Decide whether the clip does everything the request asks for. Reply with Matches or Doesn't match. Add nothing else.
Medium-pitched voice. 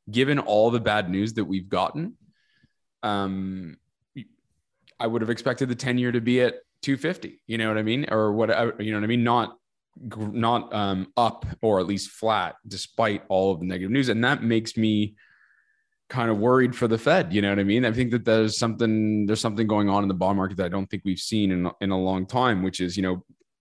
Doesn't match